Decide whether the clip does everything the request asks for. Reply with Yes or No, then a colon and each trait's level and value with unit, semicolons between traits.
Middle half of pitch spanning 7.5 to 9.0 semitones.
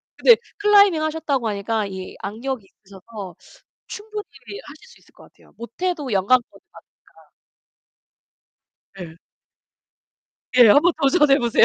Yes: wide, 8.6 semitones